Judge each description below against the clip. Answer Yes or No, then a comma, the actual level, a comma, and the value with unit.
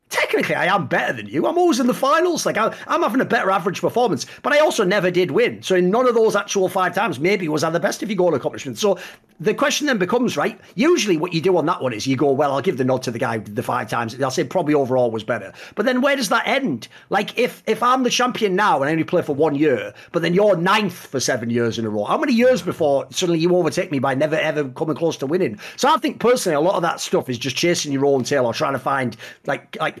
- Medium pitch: Yes, medium, 180 Hz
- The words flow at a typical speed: No, fast, 285 wpm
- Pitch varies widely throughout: Yes, wide, 8.6 semitones